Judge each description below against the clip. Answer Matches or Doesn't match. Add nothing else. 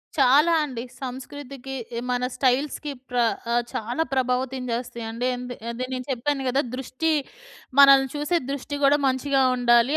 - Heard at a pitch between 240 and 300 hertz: Matches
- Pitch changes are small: Matches